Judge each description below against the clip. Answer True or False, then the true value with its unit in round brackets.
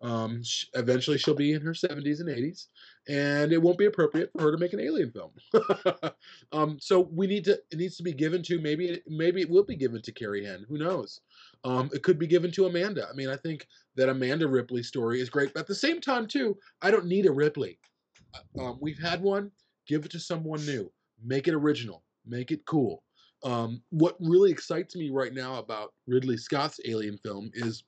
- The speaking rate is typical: False (215 wpm)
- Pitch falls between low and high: True (150 Hz)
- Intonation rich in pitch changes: True (5.8 semitones)